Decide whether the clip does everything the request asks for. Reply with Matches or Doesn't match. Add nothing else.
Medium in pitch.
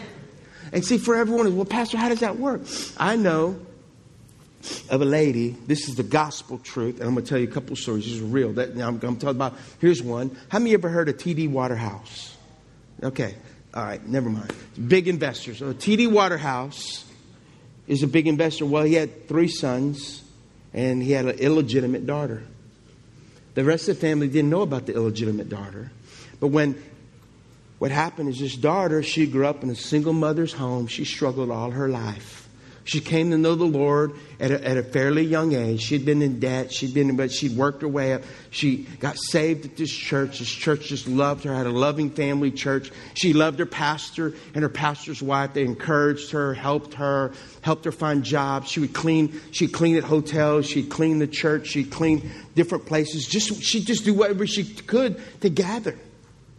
Matches